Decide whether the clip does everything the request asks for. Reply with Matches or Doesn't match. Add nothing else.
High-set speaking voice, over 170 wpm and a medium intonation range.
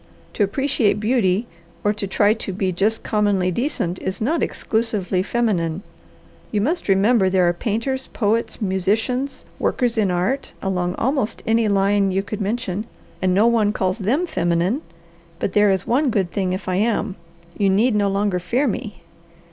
Doesn't match